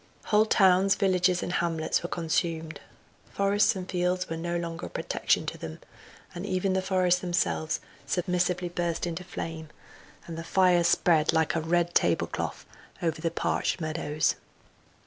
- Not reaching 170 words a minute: Yes, average, 155 wpm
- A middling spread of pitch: No, narrow, 2.0 semitones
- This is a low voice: No, medium, 175 Hz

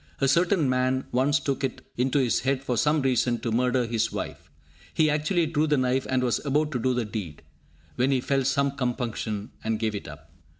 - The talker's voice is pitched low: Yes, low, 130 Hz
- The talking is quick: Yes, fast, 210 wpm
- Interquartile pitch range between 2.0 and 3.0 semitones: Yes, narrow, 2.5 semitones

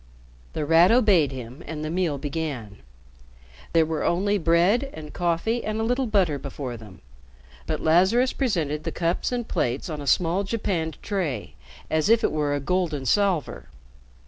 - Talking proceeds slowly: No, average, 165 wpm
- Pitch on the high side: No, medium, 165 Hz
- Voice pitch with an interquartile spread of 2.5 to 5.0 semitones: No, wide, 5.4 semitones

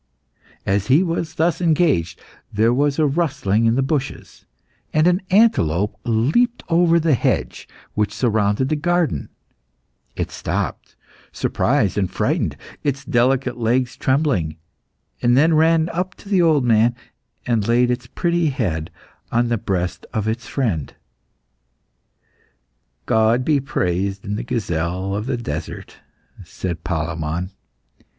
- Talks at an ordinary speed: No, slow, 130 wpm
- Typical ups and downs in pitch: No, wide, 7.3 semitones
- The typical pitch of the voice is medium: No, low, 120 Hz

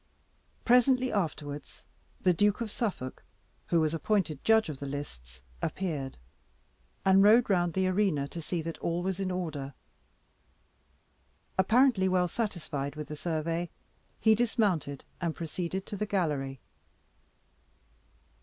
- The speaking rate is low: Yes, slow, 125 wpm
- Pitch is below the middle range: No, medium, 175 Hz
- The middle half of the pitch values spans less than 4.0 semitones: No, average, 5.2 semitones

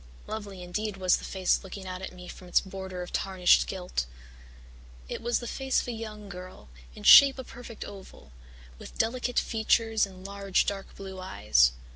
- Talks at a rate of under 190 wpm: Yes, average, 180 wpm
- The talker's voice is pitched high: Yes, high, 195 Hz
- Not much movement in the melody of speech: No, average, 3.1 semitones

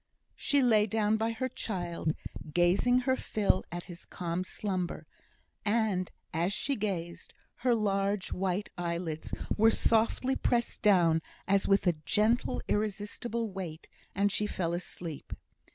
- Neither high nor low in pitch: No, high, 200 Hz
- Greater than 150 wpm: No, slow, 135 wpm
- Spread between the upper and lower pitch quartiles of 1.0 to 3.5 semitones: No, average, 4.1 semitones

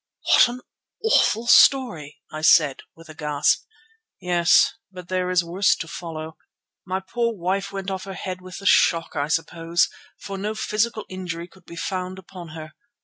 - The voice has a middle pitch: Yes, medium, 180 Hz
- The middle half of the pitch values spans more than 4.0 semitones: No, average, 2.9 semitones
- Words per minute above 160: Yes, average, 170 wpm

